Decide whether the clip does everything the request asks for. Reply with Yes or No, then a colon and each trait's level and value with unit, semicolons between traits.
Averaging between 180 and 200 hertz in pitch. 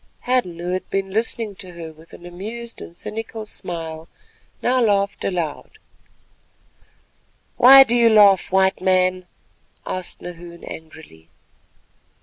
Yes: medium, 185 Hz